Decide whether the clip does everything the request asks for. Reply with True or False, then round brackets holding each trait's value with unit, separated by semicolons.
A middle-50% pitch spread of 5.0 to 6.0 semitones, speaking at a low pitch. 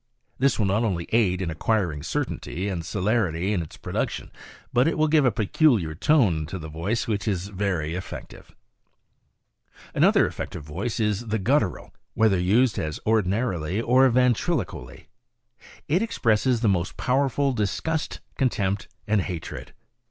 True (5.4 semitones; 105 Hz)